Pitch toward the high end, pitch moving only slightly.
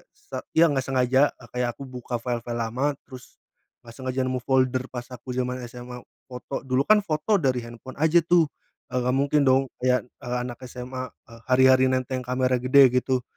No: low, 130 Hz; narrow, 1.2 semitones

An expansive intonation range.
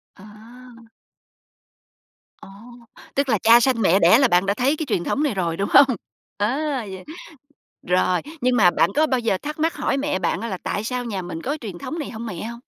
Yes: wide, 5.7 semitones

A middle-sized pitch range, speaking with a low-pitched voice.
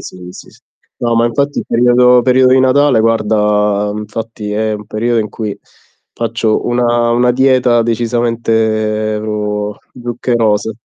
No: narrow, 2.2 semitones; low, 115 Hz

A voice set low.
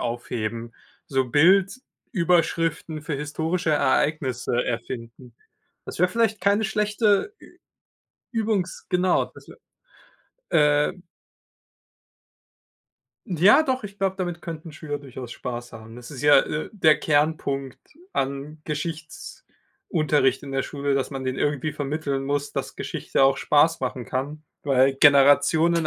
No: medium, 150 Hz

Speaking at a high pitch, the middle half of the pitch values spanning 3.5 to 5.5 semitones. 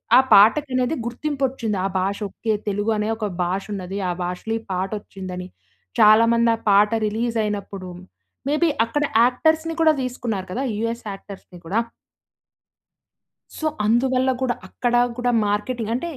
Yes: high, 225 Hz; average, 4.0 semitones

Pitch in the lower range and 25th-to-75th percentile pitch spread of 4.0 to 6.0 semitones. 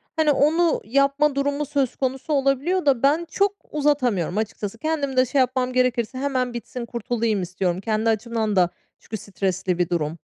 No: very high, 255 Hz; average, 4.7 semitones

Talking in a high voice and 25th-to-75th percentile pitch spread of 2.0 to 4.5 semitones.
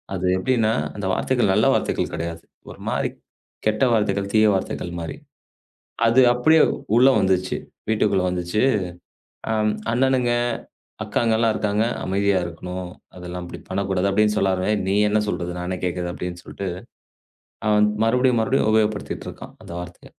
No: low, 100 Hz; average, 3.5 semitones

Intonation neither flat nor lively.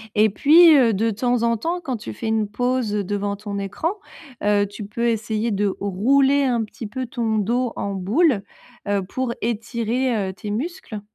Yes: average, 3.7 semitones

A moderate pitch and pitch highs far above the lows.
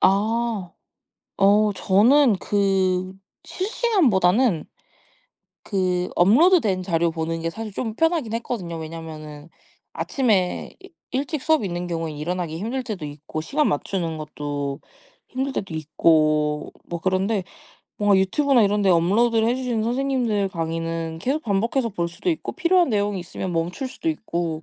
No: high, 195 Hz; wide, 6.2 semitones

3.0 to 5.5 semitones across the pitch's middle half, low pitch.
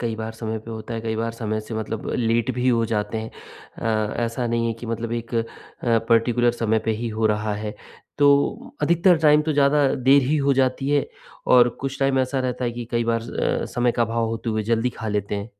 No: narrow, 2.6 semitones; low, 115 Hz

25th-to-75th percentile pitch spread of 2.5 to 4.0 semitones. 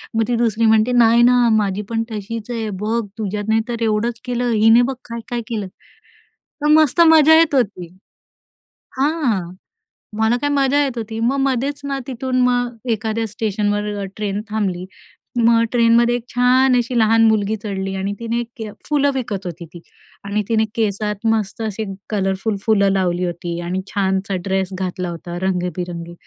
Yes: average, 3.6 semitones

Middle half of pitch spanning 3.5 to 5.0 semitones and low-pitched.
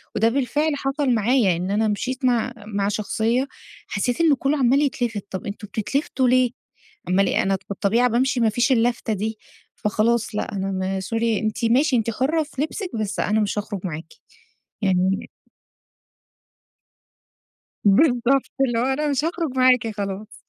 No: average, 4.2 semitones; high, 230 Hz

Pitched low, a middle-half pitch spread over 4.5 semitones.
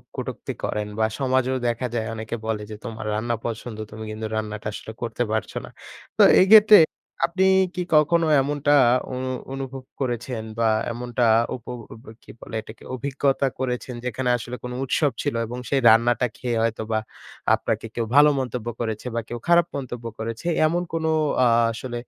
No: low, 125 Hz; average, 3.2 semitones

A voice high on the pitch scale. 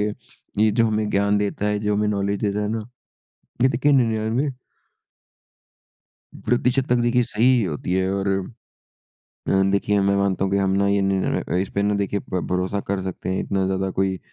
No: low, 100 Hz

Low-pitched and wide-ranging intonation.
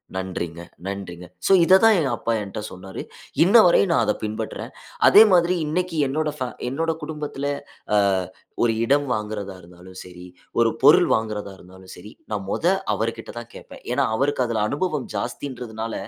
Yes: low, 115 Hz; wide, 7.4 semitones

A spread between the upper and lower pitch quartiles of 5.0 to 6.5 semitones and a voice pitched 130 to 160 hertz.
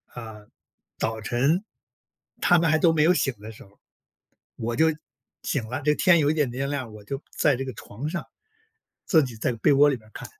Yes: average, 5.3 semitones; low, 135 Hz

